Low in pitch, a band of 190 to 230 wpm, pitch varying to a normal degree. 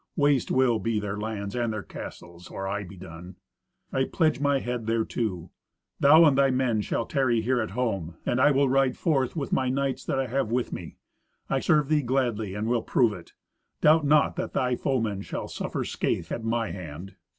Yes: low, 120 Hz; average, 200 wpm; average, 4.6 semitones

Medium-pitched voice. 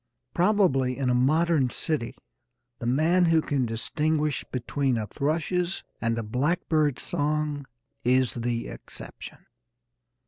Yes: medium, 145 Hz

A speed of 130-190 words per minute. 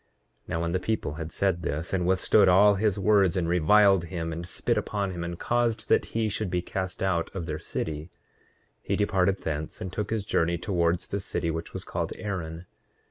No: fast, 205 wpm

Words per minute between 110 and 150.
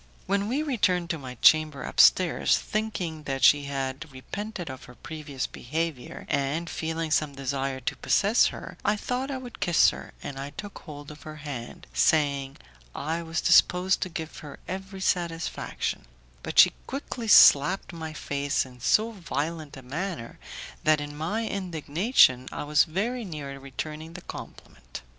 No: average, 160 wpm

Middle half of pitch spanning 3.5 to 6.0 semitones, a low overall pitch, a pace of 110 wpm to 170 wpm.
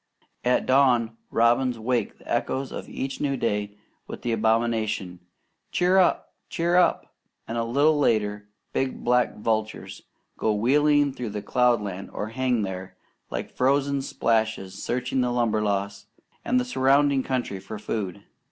Yes: average, 4.0 semitones; low, 120 Hz; average, 140 wpm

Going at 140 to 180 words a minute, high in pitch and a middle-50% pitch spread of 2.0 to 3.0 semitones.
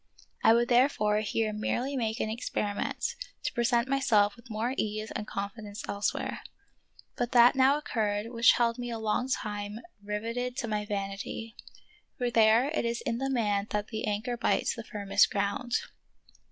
Yes: average, 170 wpm; high, 225 Hz; narrow, 2.5 semitones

